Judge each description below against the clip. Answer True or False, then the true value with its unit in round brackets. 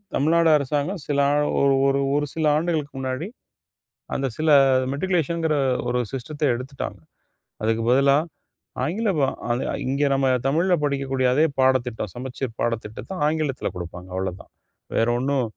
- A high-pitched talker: False (140 Hz)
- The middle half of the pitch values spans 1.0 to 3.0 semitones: False (3.6 semitones)